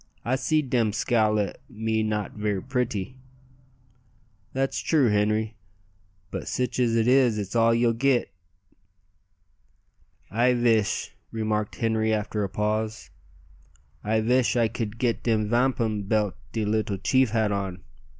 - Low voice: Yes, low, 110 Hz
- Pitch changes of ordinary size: No, narrow, 2.3 semitones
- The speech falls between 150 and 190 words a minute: No, slow, 135 wpm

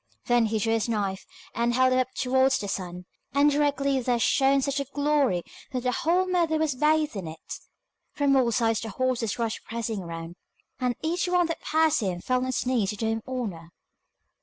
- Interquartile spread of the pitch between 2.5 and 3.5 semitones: No, average, 4.3 semitones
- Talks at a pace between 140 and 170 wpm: No, fast, 205 wpm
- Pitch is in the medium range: No, very high, 255 Hz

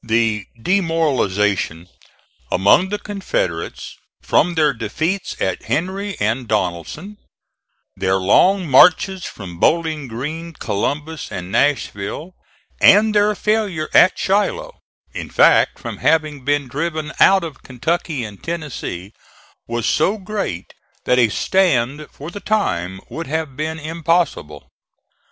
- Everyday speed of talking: No, slow, 120 wpm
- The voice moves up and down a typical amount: No, wide, 8.1 semitones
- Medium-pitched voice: Yes, medium, 150 Hz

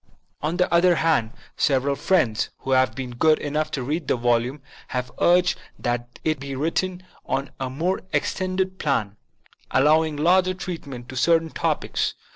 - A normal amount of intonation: Yes, average, 4.9 semitones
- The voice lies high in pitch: No, medium, 150 Hz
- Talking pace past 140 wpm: Yes, average, 160 wpm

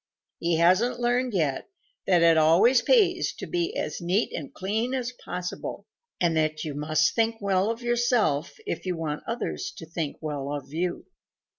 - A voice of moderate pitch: Yes, medium, 180 Hz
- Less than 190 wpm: Yes, average, 170 wpm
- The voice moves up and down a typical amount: No, wide, 7.1 semitones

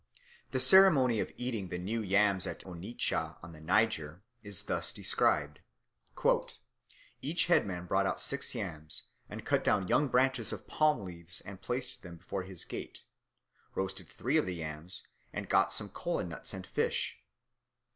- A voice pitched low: Yes, very low, 95 Hz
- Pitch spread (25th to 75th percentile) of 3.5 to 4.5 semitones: No, wide, 5.6 semitones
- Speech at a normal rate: Yes, average, 155 wpm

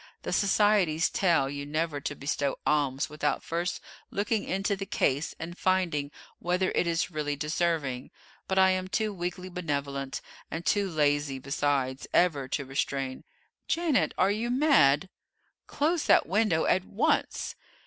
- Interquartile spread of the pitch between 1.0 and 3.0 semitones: No, average, 4.9 semitones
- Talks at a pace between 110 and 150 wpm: Yes, average, 145 wpm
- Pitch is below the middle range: No, medium, 165 Hz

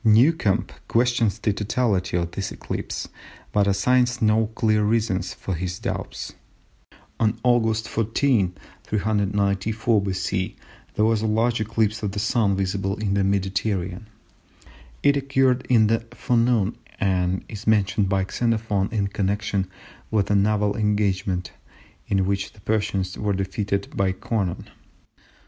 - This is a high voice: No, low, 105 Hz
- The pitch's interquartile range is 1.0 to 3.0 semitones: Yes, narrow, 2.4 semitones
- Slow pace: Yes, slow, 130 wpm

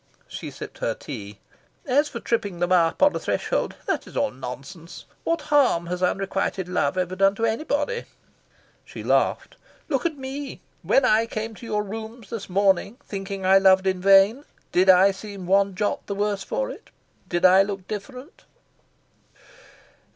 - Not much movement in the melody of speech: No, average, 3.9 semitones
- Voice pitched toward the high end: Yes, high, 200 Hz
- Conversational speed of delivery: Yes, average, 165 wpm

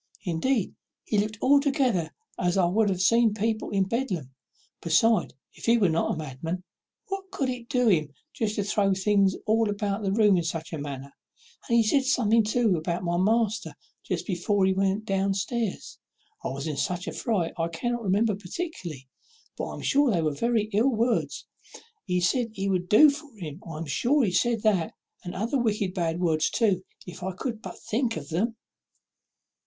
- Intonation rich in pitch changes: No, average, 4.7 semitones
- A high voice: Yes, high, 200 Hz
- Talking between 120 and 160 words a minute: No, average, 190 wpm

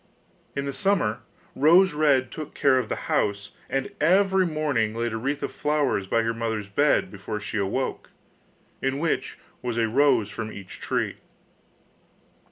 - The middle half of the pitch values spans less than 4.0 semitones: No, average, 5.3 semitones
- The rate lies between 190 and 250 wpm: No, average, 160 wpm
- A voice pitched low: Yes, low, 130 Hz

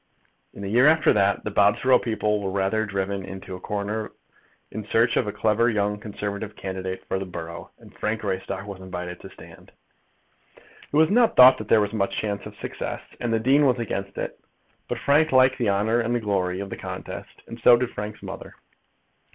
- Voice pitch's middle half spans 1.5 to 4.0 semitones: Yes, average, 3.1 semitones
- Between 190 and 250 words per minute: Yes, average, 200 wpm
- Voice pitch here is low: Yes, low, 105 Hz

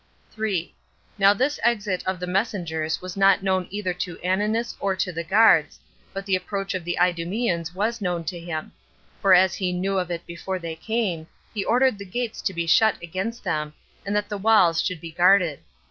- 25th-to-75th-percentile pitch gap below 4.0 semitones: Yes, average, 3.0 semitones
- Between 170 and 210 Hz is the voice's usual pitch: Yes, medium, 185 Hz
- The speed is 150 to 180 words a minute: No, average, 195 wpm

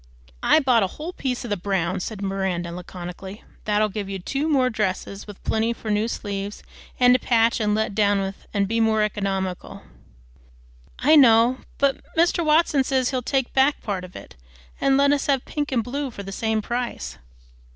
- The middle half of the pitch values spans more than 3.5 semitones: Yes, average, 4.9 semitones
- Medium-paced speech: Yes, average, 190 wpm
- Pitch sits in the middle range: No, high, 220 Hz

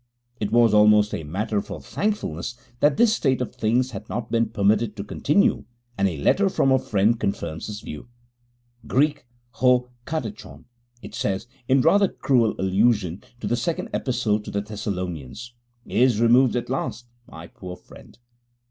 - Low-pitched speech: Yes, low, 115 Hz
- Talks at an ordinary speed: Yes, average, 160 wpm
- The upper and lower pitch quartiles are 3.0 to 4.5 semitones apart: Yes, average, 4.1 semitones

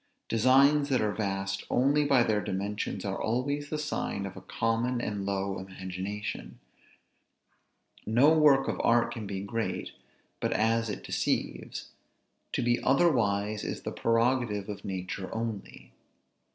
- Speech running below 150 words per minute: Yes, average, 140 wpm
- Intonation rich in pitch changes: No, average, 4.4 semitones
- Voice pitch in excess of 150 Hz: No, low, 110 Hz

